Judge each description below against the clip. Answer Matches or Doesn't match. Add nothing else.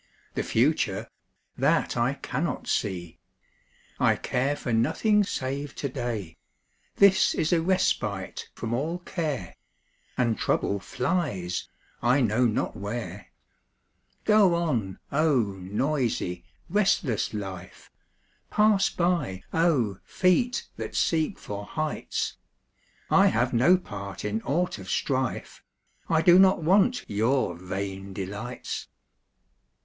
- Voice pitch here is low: Matches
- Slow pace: Matches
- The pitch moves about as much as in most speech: Doesn't match